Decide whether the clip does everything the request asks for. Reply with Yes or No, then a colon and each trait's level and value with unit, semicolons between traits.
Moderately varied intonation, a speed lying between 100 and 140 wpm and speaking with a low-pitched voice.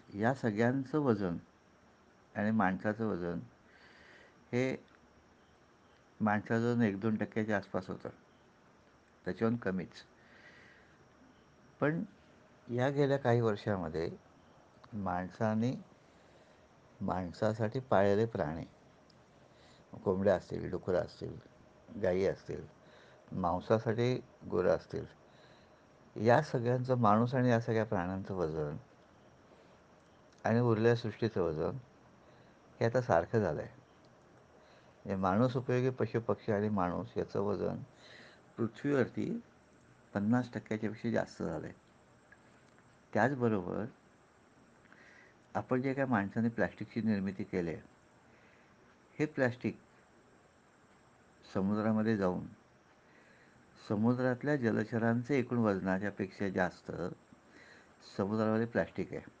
No: average, 3.2 semitones; average, 90 wpm; low, 110 Hz